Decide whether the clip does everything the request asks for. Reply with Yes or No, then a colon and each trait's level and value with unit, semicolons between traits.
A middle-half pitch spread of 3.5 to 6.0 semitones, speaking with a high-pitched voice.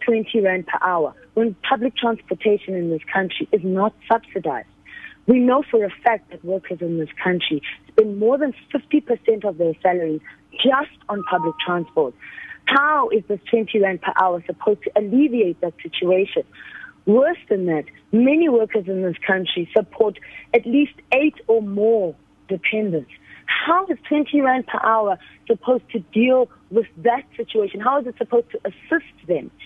Yes: wide, 5.4 semitones; high, 220 Hz